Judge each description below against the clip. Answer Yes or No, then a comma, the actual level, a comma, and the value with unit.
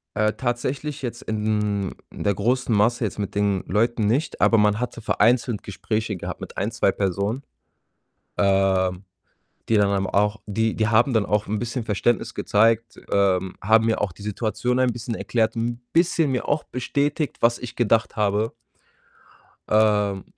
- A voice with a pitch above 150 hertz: No, low, 110 Hz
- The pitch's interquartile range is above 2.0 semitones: Yes, average, 2.7 semitones